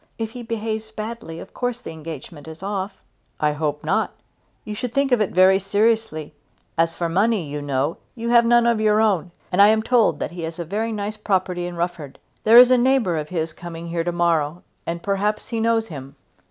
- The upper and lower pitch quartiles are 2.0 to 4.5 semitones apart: No, average, 5.2 semitones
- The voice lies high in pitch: Yes, high, 195 Hz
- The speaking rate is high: Yes, fast, 220 wpm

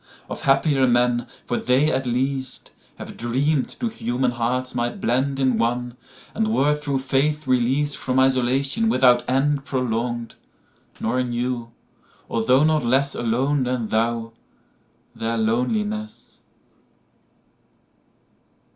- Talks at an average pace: No, slow, 95 wpm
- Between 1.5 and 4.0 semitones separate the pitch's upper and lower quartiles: Yes, narrow, 2.6 semitones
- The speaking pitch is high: No, low, 130 Hz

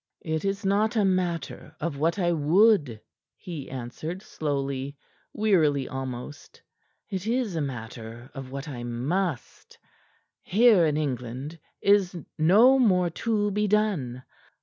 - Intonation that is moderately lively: No, wide, 6.7 semitones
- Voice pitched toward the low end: No, medium, 165 Hz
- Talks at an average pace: No, slow, 125 wpm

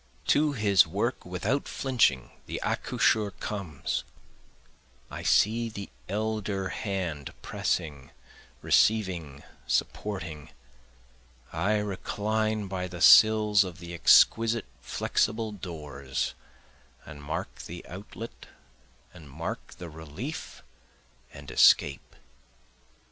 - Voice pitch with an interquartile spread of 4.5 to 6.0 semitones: Yes, average, 5.1 semitones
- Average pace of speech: No, slow, 95 wpm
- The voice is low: Yes, very low, 95 Hz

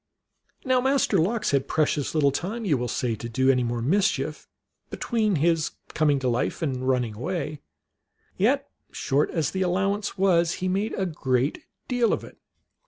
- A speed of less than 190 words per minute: Yes, average, 170 wpm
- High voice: No, medium, 160 Hz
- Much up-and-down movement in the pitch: Yes, wide, 6.8 semitones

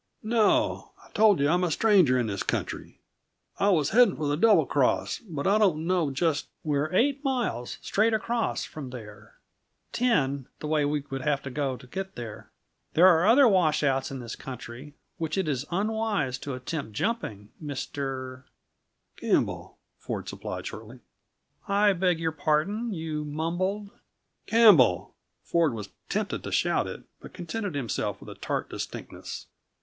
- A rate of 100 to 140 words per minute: No, average, 165 wpm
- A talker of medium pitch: Yes, medium, 155 Hz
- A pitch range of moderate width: No, wide, 7.0 semitones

